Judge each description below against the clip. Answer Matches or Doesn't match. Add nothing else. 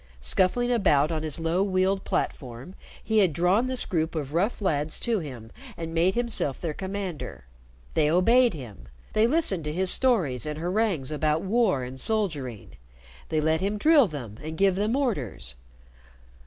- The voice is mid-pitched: Matches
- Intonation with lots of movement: Matches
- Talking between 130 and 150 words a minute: Doesn't match